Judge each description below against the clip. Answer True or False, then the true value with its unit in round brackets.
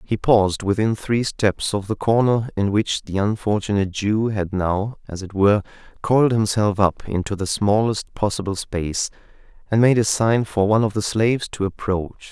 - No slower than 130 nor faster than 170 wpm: False (180 wpm)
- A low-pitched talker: True (105 Hz)